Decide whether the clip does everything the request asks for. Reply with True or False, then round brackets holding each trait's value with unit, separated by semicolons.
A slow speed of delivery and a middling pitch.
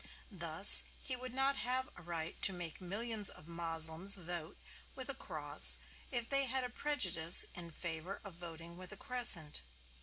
False (170 wpm; 180 Hz)